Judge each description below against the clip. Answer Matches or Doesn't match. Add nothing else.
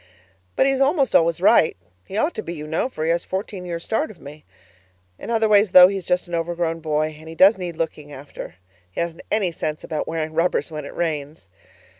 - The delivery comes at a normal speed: Doesn't match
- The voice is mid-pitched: Matches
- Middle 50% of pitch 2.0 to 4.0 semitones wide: Matches